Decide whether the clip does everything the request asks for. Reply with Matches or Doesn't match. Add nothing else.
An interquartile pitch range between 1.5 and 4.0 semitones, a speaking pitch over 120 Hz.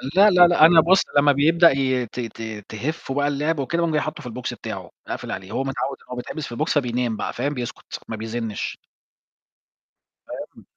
Doesn't match